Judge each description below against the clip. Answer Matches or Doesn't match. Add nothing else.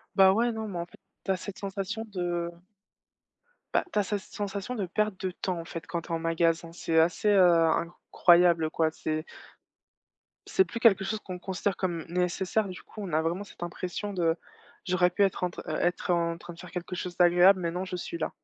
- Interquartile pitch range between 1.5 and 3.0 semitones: Matches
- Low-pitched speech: Doesn't match